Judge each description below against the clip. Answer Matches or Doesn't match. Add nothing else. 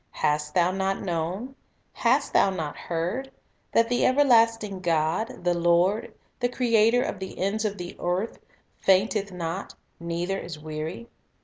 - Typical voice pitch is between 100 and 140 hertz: Doesn't match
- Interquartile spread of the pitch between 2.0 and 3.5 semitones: Doesn't match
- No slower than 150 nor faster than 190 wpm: Doesn't match